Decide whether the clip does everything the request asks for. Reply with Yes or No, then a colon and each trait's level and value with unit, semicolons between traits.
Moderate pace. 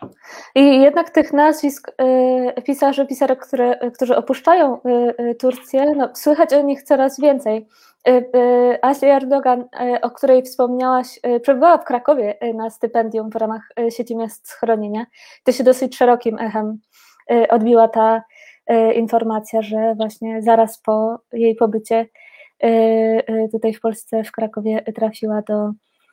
Yes: average, 150 wpm